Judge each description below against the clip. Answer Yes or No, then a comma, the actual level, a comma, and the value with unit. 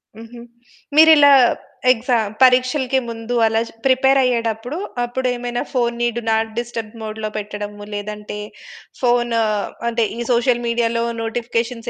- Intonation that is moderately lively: No, narrow, 1.9 semitones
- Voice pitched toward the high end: Yes, high, 235 Hz